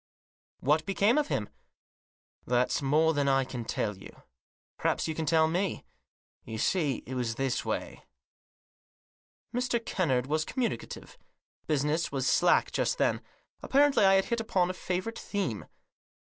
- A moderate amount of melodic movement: No, wide, 6.4 semitones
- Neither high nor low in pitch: Yes, medium, 160 Hz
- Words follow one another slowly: No, average, 155 wpm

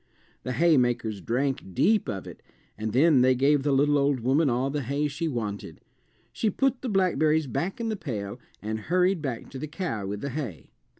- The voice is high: No, medium, 140 Hz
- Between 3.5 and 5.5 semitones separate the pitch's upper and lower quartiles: Yes, average, 5.1 semitones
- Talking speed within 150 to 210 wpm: Yes, average, 195 wpm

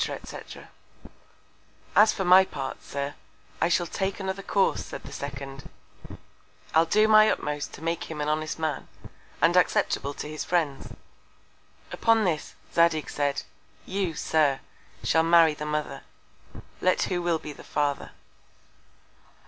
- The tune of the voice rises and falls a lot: No, average, 3.8 semitones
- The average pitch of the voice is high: No, medium, 160 Hz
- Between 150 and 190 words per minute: No, average, 140 wpm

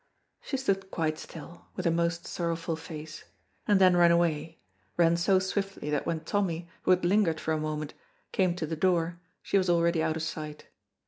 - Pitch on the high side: No, medium, 170 Hz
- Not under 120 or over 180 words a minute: No, average, 190 wpm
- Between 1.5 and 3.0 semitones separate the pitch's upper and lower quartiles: Yes, narrow, 2.4 semitones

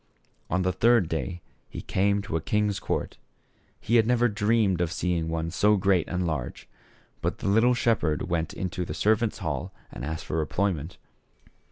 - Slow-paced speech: No, average, 175 wpm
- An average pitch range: Yes, average, 4.4 semitones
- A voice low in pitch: Yes, very low, 95 Hz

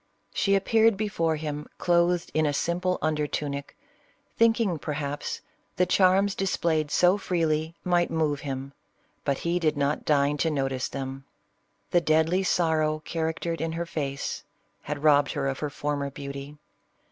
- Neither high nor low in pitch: Yes, medium, 155 Hz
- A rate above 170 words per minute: No, average, 155 wpm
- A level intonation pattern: No, average, 3.4 semitones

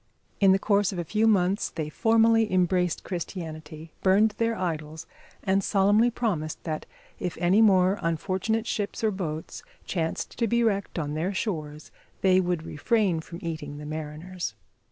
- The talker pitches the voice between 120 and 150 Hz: No, medium, 185 Hz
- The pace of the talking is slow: No, average, 155 wpm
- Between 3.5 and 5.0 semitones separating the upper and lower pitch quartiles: Yes, average, 4.5 semitones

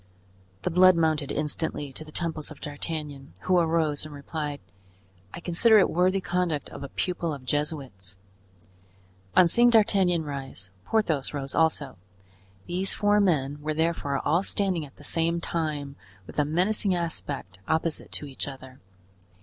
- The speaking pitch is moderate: Yes, medium, 160 Hz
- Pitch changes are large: No, average, 3.5 semitones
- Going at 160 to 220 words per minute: No, average, 150 wpm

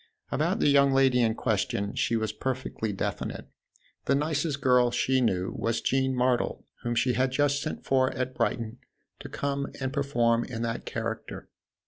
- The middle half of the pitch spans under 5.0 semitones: Yes, average, 2.7 semitones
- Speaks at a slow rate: No, average, 165 wpm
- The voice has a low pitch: Yes, low, 125 Hz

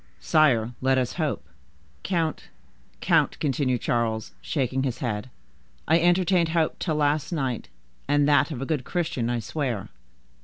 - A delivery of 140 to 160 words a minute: Yes, average, 145 wpm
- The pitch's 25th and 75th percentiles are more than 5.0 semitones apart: No, average, 4.5 semitones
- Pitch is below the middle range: No, medium, 145 Hz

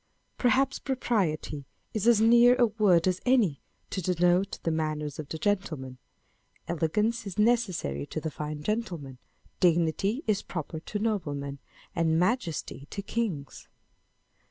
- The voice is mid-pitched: Yes, medium, 180 Hz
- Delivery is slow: Yes, slow, 130 wpm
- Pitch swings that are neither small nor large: No, wide, 6.0 semitones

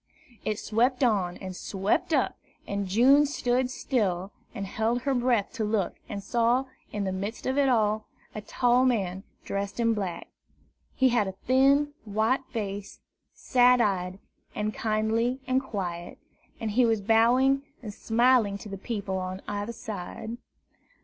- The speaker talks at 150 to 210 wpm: Yes, average, 155 wpm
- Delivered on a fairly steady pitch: No, average, 3.8 semitones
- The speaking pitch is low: No, high, 220 Hz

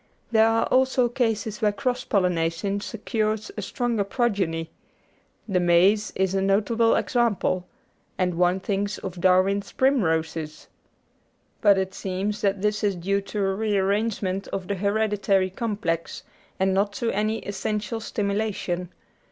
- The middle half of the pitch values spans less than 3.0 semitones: Yes, narrow, 2.5 semitones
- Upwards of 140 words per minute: No, slow, 135 wpm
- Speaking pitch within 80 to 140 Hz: No, high, 200 Hz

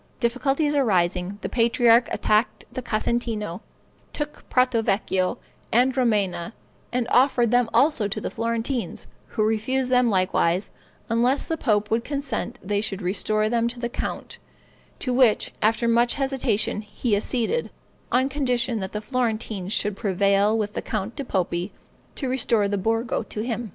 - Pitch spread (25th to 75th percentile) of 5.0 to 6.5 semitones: No, average, 3.2 semitones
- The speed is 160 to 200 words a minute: No, average, 150 wpm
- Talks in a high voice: Yes, high, 230 Hz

